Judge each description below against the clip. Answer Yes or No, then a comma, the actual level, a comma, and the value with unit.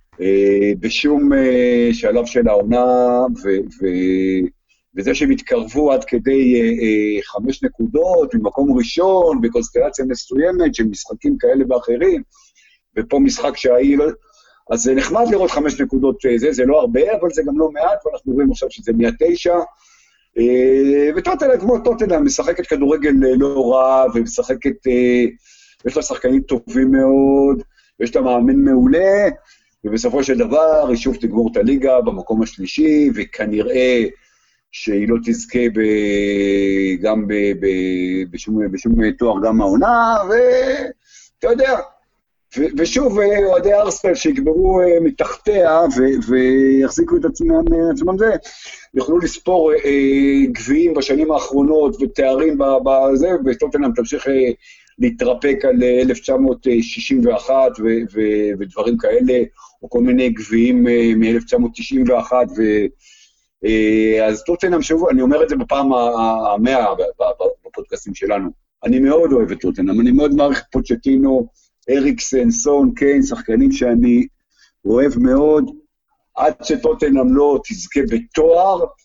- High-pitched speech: No, medium, 140 Hz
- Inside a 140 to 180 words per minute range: No, average, 125 wpm